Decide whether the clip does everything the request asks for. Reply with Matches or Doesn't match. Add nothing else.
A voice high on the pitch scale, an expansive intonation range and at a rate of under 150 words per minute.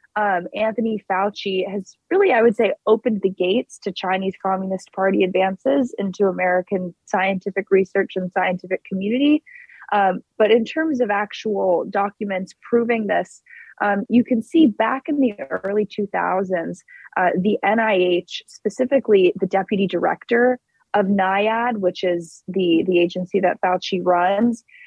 Doesn't match